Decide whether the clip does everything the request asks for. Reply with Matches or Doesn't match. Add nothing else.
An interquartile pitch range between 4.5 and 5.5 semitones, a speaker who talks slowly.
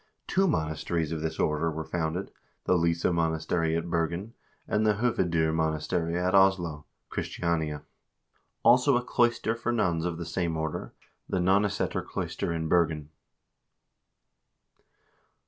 Doesn't match